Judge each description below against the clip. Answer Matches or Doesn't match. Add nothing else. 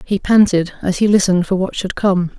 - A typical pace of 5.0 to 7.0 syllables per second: Matches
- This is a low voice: Doesn't match